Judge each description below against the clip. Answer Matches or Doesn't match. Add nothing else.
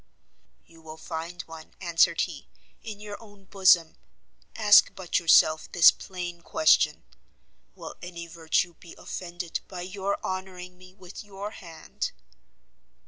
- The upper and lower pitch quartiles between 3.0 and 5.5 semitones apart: Doesn't match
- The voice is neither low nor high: Matches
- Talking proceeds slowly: Matches